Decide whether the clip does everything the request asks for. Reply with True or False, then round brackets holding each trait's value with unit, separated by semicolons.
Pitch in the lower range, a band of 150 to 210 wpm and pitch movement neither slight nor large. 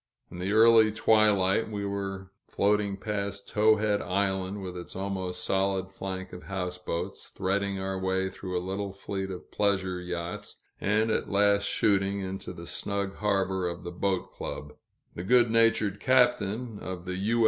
False (95 Hz; 160 wpm; 1.7 semitones)